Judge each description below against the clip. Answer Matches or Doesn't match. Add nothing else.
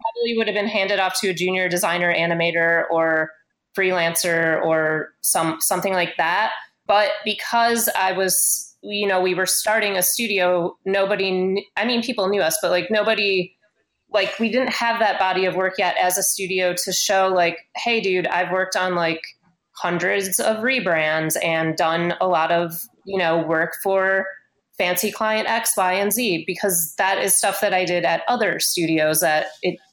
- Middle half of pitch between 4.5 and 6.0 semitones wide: Doesn't match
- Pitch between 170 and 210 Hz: Matches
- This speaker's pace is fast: Doesn't match